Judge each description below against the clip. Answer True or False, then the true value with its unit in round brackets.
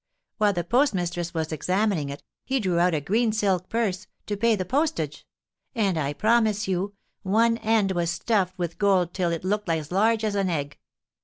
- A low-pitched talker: False (190 Hz)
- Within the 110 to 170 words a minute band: False (185 wpm)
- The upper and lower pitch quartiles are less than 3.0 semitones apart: False (3.8 semitones)